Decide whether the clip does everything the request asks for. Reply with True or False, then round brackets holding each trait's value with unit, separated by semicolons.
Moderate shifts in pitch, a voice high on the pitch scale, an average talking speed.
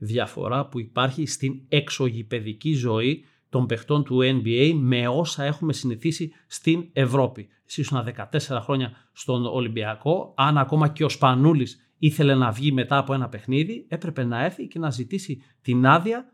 False (3.6 semitones; 135 Hz; 150 wpm)